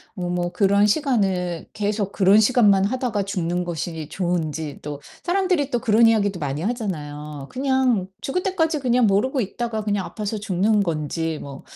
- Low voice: No, high, 200 Hz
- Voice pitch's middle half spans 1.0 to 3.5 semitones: No, wide, 5.4 semitones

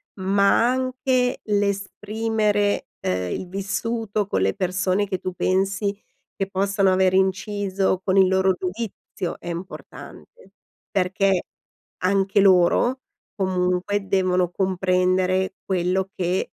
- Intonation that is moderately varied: No, narrow, 1.7 semitones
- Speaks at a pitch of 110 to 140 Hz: No, high, 190 Hz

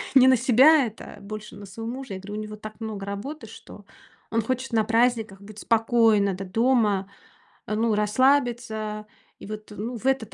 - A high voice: Yes, high, 220 Hz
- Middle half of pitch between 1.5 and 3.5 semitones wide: Yes, narrow, 2.6 semitones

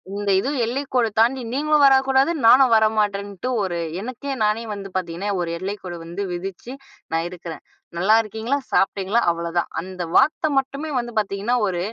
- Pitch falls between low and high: No, high, 210 Hz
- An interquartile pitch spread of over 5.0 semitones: Yes, wide, 5.6 semitones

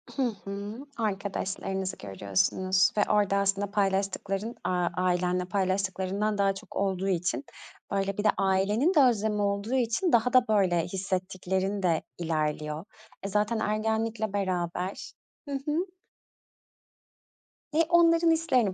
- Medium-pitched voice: No, high, 195 Hz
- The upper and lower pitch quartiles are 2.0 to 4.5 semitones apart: Yes, average, 2.7 semitones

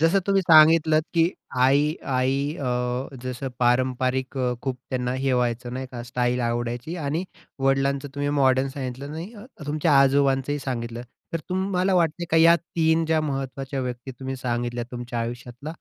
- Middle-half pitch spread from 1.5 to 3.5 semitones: No, average, 3.9 semitones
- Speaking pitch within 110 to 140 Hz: Yes, low, 135 Hz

